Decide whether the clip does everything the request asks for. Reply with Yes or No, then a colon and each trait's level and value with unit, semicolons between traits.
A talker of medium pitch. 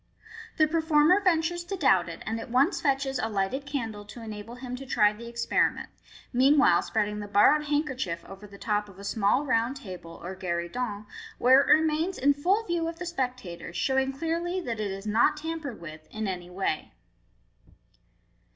No: high, 245 Hz